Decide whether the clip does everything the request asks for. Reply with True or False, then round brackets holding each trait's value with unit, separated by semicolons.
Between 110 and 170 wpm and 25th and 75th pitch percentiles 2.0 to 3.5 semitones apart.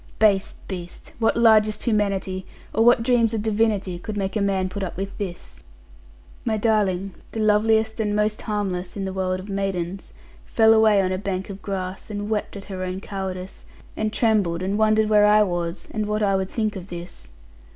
False (195 wpm; 2.4 semitones)